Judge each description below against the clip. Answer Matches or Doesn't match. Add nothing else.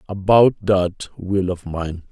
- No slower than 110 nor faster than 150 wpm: Matches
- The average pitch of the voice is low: Matches